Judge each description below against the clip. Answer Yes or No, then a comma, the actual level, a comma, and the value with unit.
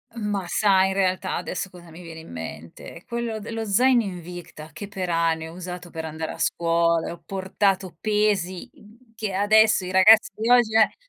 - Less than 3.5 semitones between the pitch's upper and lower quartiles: No, average, 4.0 semitones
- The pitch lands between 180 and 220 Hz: Yes, high, 190 Hz